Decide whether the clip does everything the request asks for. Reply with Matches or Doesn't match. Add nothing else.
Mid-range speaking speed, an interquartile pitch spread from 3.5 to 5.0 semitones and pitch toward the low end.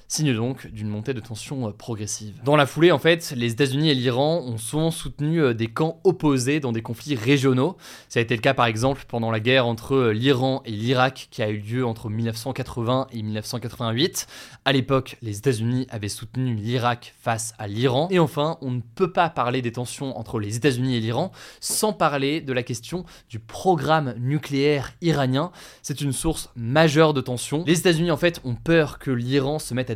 Matches